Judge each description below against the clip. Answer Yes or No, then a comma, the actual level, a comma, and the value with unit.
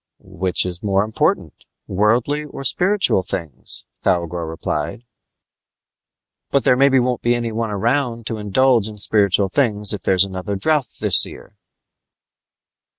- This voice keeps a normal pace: No, slow, 130 wpm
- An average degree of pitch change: Yes, average, 4.7 semitones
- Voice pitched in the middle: No, low, 110 Hz